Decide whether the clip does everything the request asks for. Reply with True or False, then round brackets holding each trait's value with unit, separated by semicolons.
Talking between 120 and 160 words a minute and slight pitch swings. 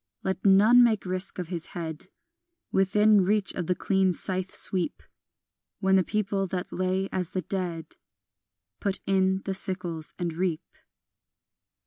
True (140 wpm; 1.4 semitones)